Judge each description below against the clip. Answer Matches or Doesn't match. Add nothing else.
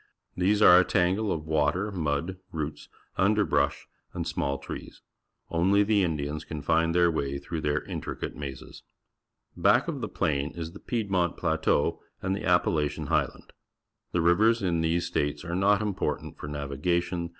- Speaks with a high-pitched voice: Doesn't match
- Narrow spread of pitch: Doesn't match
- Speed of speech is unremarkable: Matches